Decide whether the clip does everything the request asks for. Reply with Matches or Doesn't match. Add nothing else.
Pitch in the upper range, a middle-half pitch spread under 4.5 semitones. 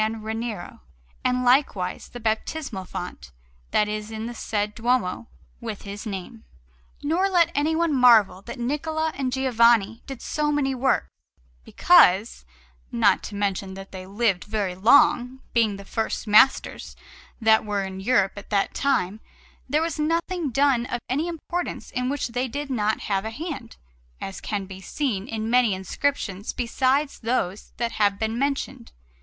Doesn't match